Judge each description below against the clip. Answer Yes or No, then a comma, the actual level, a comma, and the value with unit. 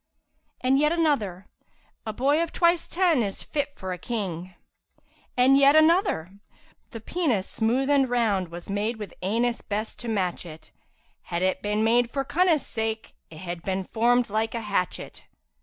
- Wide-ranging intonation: Yes, wide, 6.1 semitones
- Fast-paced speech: No, average, 165 wpm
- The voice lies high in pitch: Yes, high, 225 Hz